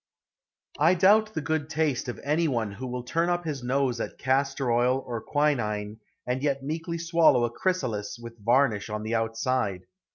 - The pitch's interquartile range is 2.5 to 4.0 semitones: No, average, 5.0 semitones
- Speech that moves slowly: No, average, 175 wpm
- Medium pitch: No, low, 130 Hz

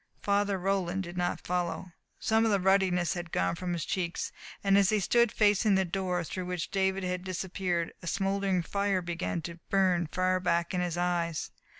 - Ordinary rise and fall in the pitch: No, narrow, 1.9 semitones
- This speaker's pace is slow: No, average, 190 wpm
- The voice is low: No, medium, 185 Hz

